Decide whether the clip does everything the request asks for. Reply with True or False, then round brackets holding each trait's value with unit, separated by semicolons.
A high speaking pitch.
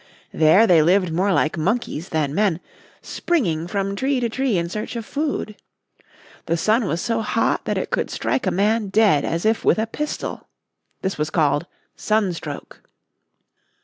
True (195 Hz)